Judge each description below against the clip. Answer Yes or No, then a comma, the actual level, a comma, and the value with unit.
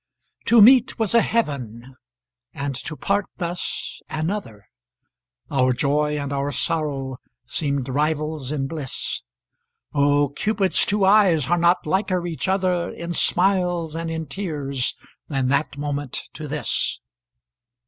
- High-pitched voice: No, medium, 155 Hz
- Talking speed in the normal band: No, slow, 130 wpm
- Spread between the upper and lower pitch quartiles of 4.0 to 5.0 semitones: Yes, average, 4.3 semitones